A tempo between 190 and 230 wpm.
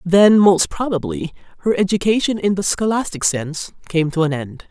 No: average, 165 wpm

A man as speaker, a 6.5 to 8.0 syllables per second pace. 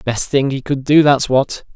No: male; 4.4 syllables/s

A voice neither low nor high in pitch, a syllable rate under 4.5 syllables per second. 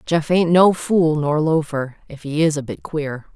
Yes: medium, 155 Hz; 4.2 syllables/s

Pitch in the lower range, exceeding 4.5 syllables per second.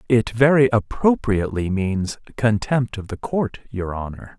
No: low, 110 Hz; 4.4 syllables/s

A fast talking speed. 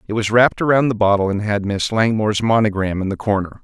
Yes: fast, 230 wpm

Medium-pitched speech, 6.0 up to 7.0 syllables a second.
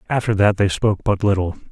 No: low, 100 Hz; 6.4 syllables/s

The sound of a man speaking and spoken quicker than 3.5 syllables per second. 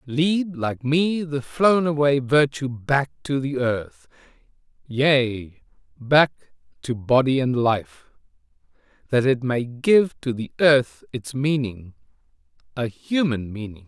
No: male; 3.4 syllables/s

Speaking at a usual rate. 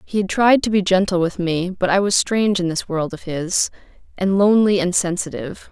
No: fast, 220 wpm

